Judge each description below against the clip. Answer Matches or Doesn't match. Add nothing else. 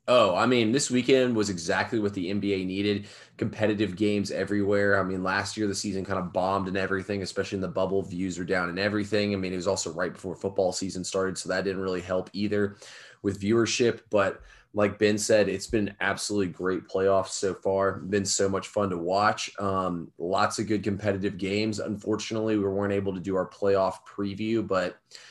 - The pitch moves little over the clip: Matches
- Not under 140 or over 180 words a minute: Doesn't match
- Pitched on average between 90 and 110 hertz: Matches